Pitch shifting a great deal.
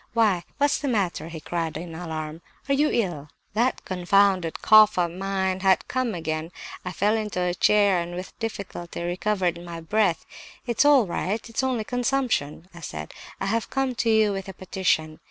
No: average, 4.3 semitones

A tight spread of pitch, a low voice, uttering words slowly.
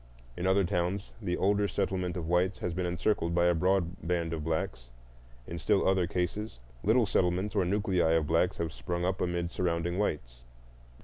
No: narrow, 2.1 semitones; very low, 90 Hz; average, 180 wpm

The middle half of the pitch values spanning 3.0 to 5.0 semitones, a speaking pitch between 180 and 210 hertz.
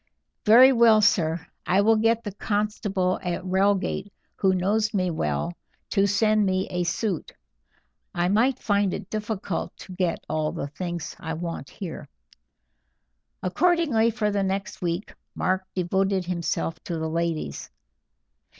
Yes: average, 3.6 semitones; high, 190 Hz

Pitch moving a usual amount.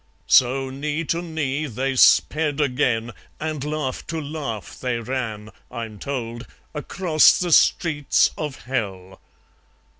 Yes: average, 4.3 semitones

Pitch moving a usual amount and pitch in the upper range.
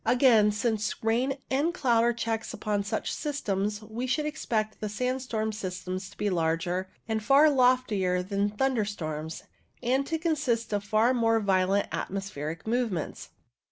Yes: average, 4.1 semitones; high, 220 Hz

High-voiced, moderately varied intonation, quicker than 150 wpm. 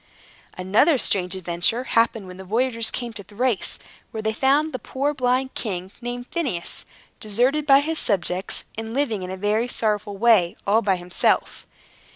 Yes: high, 225 Hz; average, 4.9 semitones; average, 165 wpm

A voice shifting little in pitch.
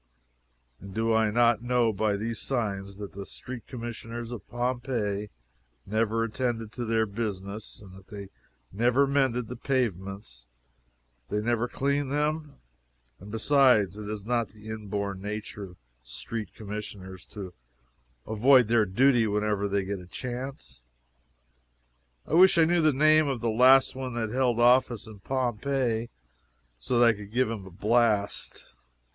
No: average, 3.5 semitones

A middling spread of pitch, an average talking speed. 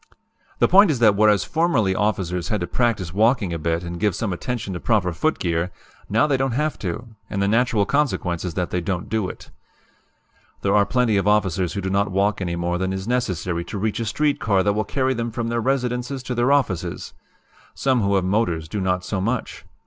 No: average, 4.7 semitones; fast, 220 wpm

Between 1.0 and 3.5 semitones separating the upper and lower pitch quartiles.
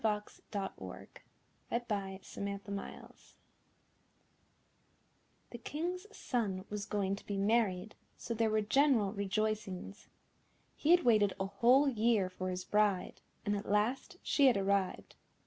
Yes: average, 3.1 semitones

